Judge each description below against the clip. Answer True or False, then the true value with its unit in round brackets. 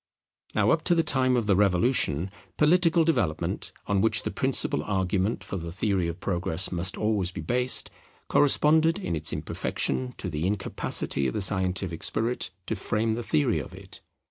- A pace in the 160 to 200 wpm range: True (170 wpm)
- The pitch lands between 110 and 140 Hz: False (100 Hz)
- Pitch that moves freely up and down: True (5.7 semitones)